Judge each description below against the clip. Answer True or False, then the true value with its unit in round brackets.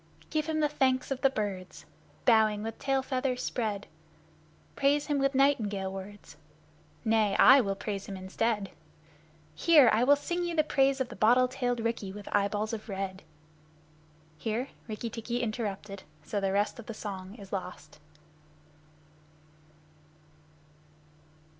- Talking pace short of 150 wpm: True (140 wpm)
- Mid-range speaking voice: False (225 Hz)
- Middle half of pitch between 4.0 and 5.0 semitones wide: True (4.7 semitones)